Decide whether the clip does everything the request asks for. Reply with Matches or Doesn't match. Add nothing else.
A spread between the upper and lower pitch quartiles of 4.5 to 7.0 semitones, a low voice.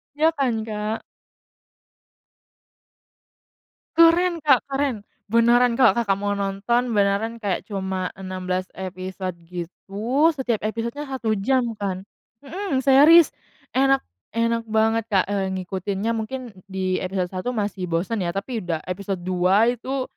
Doesn't match